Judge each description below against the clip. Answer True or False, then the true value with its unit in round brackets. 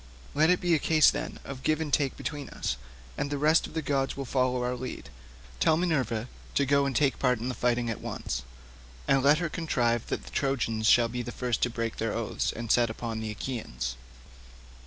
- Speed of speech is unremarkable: False (220 wpm)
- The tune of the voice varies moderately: True (3.6 semitones)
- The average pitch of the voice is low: True (130 Hz)